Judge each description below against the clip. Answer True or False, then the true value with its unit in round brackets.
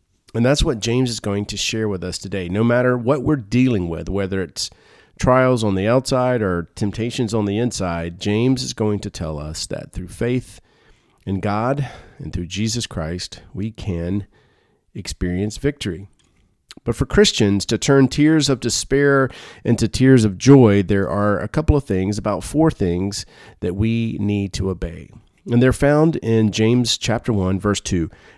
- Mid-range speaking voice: False (105 Hz)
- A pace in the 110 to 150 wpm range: False (175 wpm)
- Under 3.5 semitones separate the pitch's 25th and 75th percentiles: False (4.4 semitones)